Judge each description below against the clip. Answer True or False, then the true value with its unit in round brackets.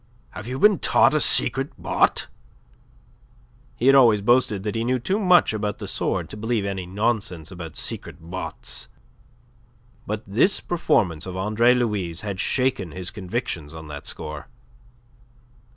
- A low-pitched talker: True (105 Hz)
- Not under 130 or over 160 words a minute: True (150 wpm)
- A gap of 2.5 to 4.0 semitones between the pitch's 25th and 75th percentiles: False (5.0 semitones)